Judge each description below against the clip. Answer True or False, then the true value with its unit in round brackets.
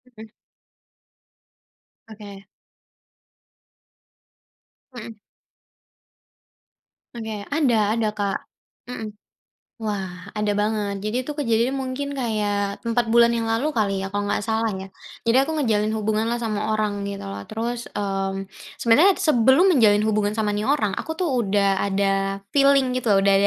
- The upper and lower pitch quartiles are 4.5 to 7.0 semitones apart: False (2.8 semitones)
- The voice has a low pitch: False (215 Hz)